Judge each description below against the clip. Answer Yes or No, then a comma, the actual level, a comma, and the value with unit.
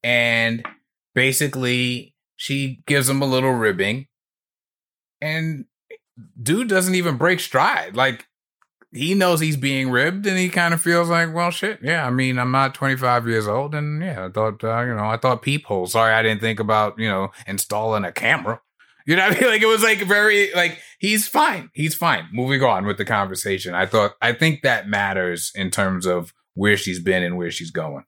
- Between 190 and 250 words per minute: Yes, average, 195 wpm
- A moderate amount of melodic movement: No, wide, 7.5 semitones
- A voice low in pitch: Yes, low, 130 Hz